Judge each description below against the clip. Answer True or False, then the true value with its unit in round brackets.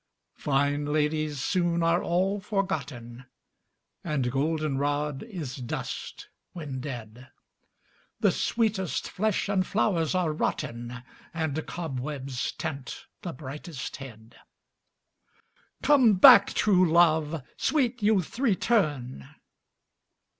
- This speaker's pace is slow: True (95 wpm)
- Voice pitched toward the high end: False (155 Hz)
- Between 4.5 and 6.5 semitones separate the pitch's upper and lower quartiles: True (5.5 semitones)